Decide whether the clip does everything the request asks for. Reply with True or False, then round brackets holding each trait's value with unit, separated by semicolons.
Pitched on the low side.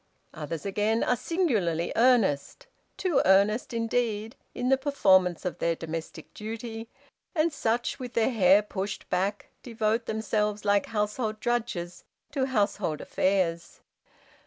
False (215 Hz)